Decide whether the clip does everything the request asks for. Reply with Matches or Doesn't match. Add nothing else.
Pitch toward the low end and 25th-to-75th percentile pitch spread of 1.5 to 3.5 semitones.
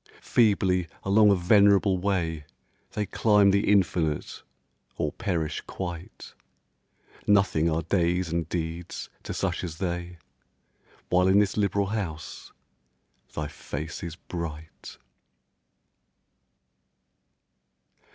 Matches